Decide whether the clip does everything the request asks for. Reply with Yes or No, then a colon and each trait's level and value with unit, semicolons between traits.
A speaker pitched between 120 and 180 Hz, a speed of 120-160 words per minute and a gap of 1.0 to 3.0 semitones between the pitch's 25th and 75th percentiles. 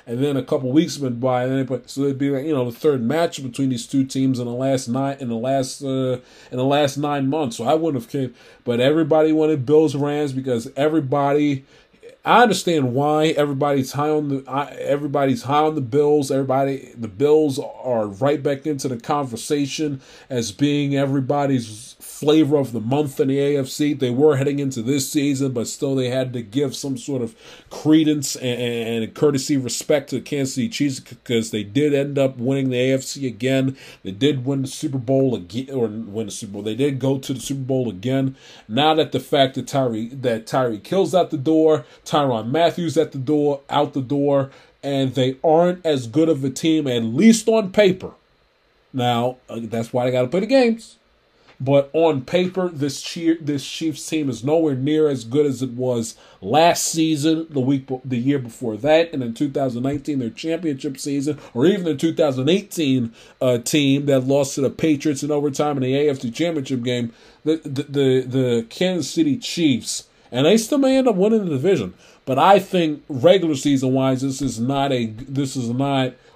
No: medium, 140 Hz; average, 200 wpm; average, 2.7 semitones